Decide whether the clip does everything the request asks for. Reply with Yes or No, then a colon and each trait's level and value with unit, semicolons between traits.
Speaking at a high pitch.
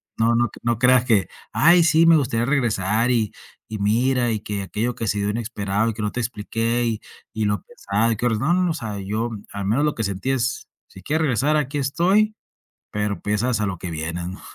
No: low, 115 Hz